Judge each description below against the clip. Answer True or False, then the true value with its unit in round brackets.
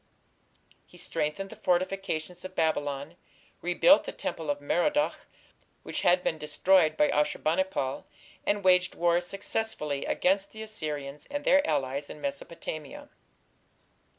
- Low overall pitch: False (175 Hz)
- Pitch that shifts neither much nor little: True (4.5 semitones)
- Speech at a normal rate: False (130 wpm)